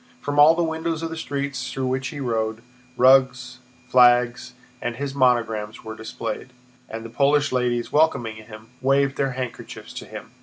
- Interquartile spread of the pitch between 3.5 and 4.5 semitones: No, average, 3.0 semitones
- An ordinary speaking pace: Yes, average, 165 wpm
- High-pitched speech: No, low, 130 Hz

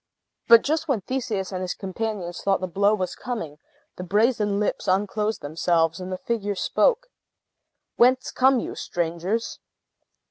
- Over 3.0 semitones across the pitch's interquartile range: Yes, average, 4.1 semitones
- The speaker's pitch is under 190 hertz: No, high, 205 Hz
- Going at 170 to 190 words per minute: No, average, 145 wpm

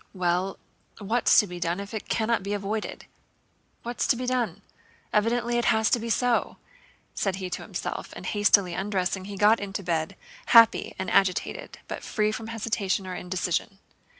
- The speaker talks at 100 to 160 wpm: No, average, 170 wpm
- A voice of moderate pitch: No, high, 205 Hz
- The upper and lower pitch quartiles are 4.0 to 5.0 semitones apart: No, average, 3.3 semitones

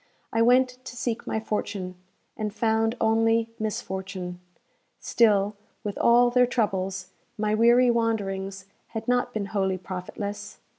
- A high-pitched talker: Yes, high, 220 Hz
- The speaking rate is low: Yes, slow, 130 wpm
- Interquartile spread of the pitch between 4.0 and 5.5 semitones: No, average, 3.2 semitones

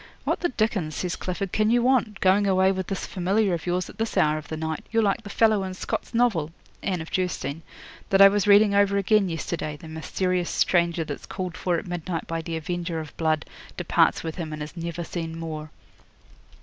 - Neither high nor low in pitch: Yes, medium, 180 Hz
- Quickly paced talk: Yes, fast, 215 wpm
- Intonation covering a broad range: No, average, 3.6 semitones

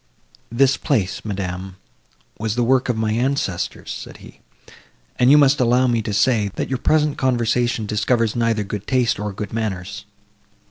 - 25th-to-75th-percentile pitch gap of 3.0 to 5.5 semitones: Yes, average, 3.5 semitones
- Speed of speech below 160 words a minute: No, average, 165 wpm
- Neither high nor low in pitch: No, low, 115 Hz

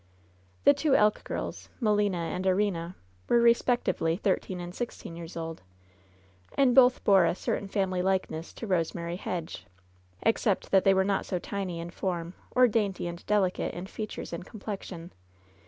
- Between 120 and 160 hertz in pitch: No, high, 190 Hz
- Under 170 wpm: Yes, average, 160 wpm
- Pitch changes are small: No, average, 3.4 semitones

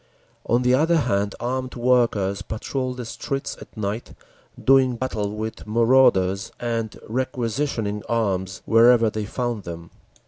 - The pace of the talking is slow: Yes, slow, 130 wpm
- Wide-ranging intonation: No, average, 3.5 semitones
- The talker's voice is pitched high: No, low, 115 Hz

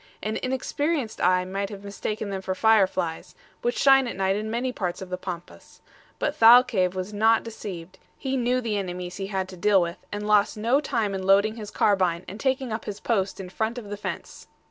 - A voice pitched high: Yes, high, 205 Hz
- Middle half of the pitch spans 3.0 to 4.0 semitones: Yes, average, 3.5 semitones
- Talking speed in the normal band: No, fast, 210 wpm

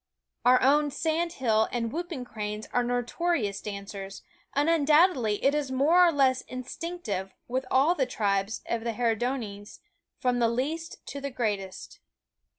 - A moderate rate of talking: Yes, average, 150 wpm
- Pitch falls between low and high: No, very high, 255 Hz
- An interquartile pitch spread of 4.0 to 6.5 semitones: Yes, average, 5.3 semitones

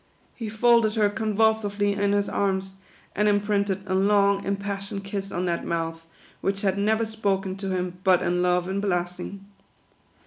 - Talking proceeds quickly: No, average, 160 wpm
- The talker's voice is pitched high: Yes, high, 200 Hz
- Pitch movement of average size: No, narrow, 1.6 semitones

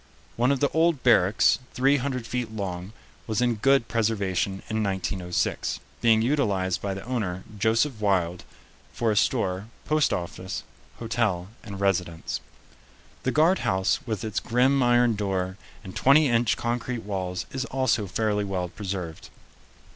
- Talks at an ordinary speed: Yes, average, 145 wpm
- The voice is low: Yes, low, 110 Hz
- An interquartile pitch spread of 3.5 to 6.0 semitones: Yes, average, 4.4 semitones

